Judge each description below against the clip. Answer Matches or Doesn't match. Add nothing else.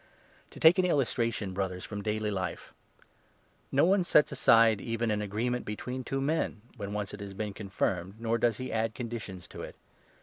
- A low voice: Matches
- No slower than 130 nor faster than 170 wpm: Doesn't match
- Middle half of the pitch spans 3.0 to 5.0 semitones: Matches